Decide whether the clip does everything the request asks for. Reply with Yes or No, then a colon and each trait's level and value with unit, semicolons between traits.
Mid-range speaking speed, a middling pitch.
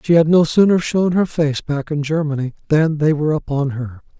No: fast, 215 wpm; medium, 155 Hz